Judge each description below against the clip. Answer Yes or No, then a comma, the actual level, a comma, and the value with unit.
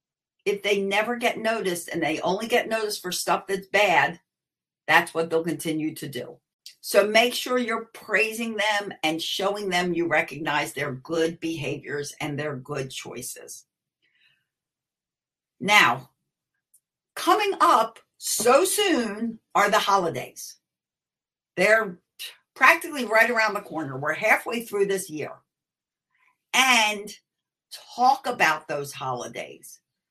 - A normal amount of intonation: No, wide, 6.0 semitones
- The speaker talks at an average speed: No, slow, 125 wpm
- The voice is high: Yes, high, 195 Hz